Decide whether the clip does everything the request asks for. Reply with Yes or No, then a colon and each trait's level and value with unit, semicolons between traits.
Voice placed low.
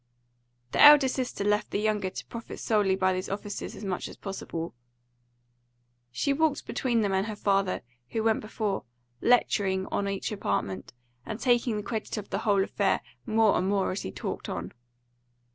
No: high, 205 Hz